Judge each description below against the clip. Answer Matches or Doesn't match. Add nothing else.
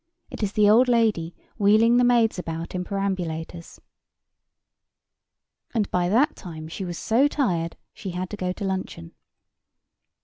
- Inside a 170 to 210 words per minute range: Doesn't match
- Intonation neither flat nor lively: Matches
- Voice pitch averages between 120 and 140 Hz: Doesn't match